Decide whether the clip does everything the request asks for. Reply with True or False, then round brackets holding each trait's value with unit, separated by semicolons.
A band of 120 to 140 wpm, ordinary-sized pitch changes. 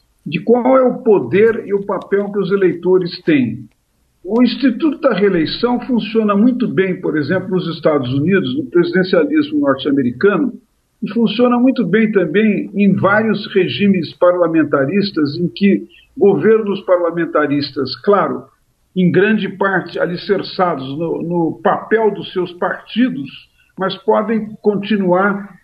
True (125 wpm; 3.9 semitones)